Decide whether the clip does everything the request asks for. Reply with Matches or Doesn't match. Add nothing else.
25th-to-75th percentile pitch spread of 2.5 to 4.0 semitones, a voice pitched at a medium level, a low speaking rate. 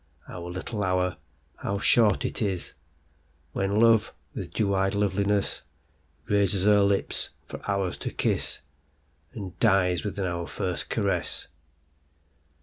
Doesn't match